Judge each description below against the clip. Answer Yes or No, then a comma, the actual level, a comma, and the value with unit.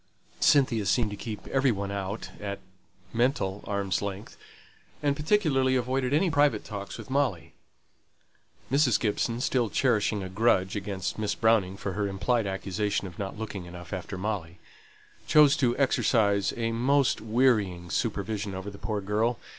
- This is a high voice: No, low, 105 Hz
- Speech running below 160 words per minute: Yes, average, 150 wpm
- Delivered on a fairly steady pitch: No, average, 4.1 semitones